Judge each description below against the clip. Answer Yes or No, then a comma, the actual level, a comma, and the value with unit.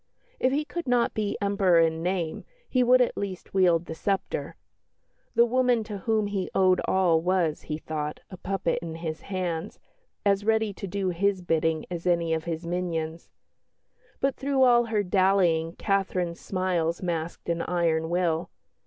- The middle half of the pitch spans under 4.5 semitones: Yes, average, 3.5 semitones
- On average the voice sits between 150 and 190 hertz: Yes, medium, 185 Hz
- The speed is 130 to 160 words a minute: No, average, 170 wpm